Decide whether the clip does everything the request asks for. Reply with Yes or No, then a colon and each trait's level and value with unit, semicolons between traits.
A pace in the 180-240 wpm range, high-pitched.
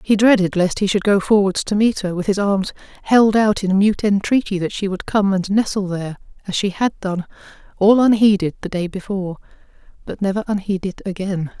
Yes: average, 195 wpm; high, 200 Hz